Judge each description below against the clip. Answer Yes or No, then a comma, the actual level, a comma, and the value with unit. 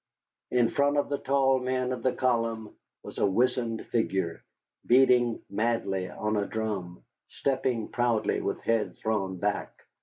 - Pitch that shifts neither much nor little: Yes, average, 3.3 semitones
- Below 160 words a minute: Yes, average, 145 wpm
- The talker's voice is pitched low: Yes, low, 115 Hz